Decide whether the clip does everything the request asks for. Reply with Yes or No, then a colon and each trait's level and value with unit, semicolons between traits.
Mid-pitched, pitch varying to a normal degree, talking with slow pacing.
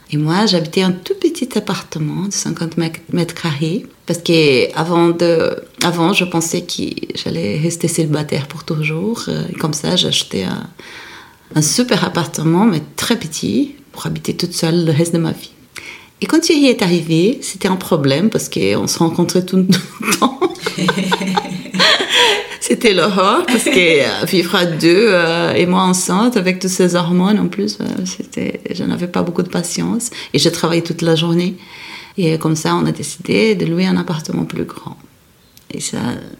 No: medium, 180 Hz; average, 4.2 semitones; average, 170 wpm